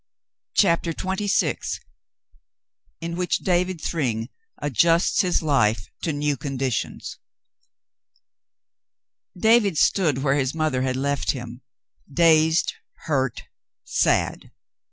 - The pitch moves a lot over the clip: No, average, 4.5 semitones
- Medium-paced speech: No, slow, 90 wpm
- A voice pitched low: No, medium, 155 Hz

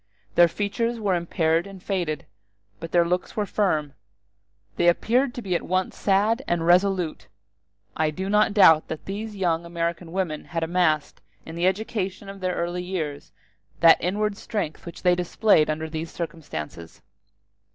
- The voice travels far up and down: No, average, 3.2 semitones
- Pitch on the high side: No, medium, 180 Hz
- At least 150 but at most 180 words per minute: Yes, average, 160 wpm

